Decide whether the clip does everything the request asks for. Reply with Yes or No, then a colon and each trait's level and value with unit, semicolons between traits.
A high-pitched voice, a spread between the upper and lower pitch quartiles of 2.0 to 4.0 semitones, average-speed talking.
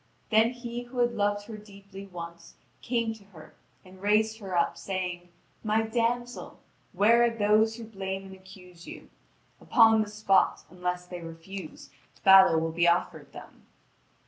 Yes: high, 200 Hz; average, 3.7 semitones; average, 155 wpm